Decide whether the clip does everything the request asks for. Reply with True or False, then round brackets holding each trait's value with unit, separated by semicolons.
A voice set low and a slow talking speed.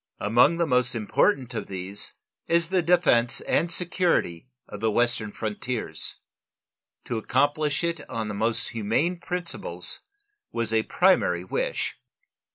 True (120 Hz; 130 wpm)